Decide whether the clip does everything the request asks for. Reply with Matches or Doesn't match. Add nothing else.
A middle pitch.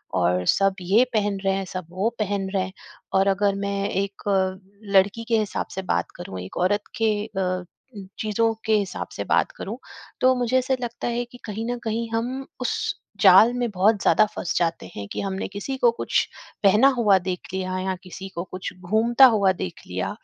Doesn't match